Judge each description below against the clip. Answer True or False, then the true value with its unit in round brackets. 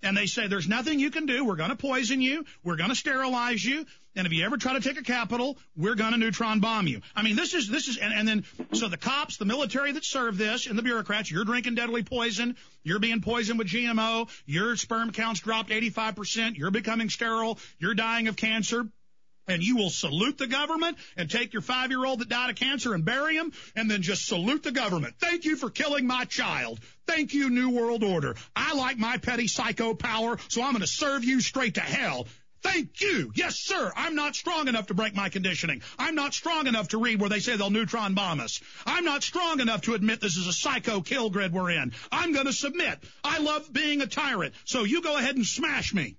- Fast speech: True (230 wpm)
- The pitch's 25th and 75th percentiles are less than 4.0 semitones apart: False (4.3 semitones)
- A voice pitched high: True (235 Hz)